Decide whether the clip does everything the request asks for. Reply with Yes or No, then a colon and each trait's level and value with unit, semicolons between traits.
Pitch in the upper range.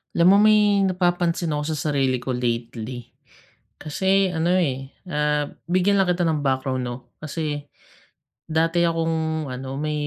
No: medium, 160 Hz